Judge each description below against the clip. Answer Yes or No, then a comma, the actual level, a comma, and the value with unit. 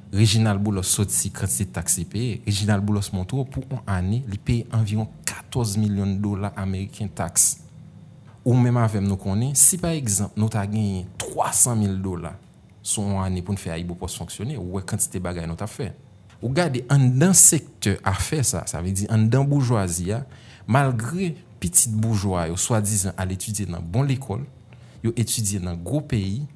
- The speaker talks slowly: No, average, 180 wpm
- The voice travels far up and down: No, average, 4.0 semitones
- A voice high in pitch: No, low, 105 Hz